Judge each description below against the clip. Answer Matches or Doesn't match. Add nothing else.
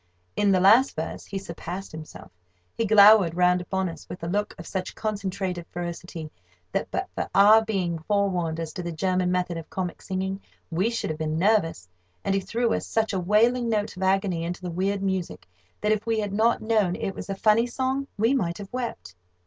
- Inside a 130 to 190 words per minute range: Doesn't match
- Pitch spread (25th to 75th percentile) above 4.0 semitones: Doesn't match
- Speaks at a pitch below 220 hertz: Matches